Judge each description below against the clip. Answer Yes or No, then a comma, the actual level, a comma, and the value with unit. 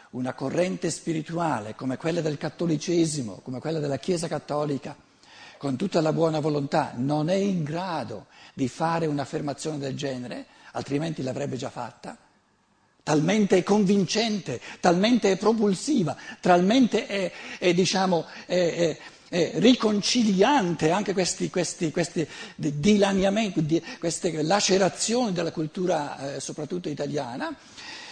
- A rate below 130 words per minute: Yes, average, 120 wpm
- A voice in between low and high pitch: Yes, medium, 170 Hz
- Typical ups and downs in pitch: Yes, average, 4.8 semitones